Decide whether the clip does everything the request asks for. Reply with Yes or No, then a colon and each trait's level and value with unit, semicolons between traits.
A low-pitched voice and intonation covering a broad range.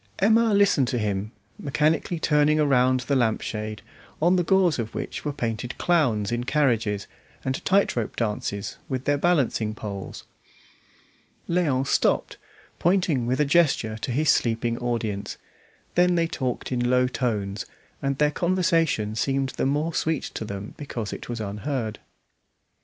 Yes: low, 130 Hz; wide, 5.7 semitones